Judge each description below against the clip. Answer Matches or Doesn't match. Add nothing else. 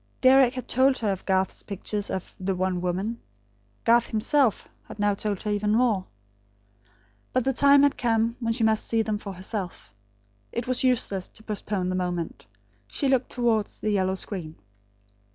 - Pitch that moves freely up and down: Doesn't match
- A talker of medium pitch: Doesn't match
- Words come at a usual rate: Matches